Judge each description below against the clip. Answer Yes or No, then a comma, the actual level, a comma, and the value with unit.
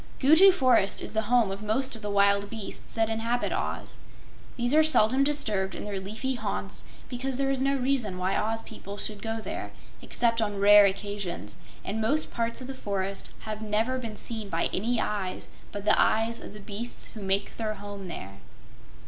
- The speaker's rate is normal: Yes, average, 190 wpm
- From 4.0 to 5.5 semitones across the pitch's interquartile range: No, average, 3.4 semitones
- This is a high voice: Yes, high, 220 Hz